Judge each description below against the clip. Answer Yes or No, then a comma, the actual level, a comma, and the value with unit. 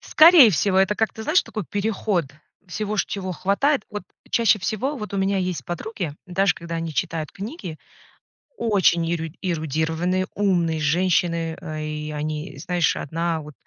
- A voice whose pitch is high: No, medium, 180 Hz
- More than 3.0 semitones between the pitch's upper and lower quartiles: Yes, average, 4.0 semitones